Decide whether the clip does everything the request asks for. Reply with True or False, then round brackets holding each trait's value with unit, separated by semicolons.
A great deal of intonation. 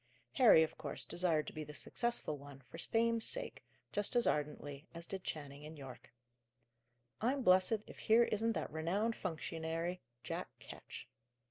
True (6.8 semitones)